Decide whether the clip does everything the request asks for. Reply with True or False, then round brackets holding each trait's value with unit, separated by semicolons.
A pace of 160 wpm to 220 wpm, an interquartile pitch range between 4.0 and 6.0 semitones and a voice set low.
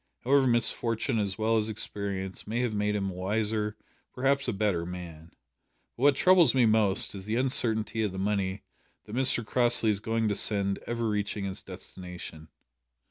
False (175 wpm; 3.2 semitones; 105 Hz)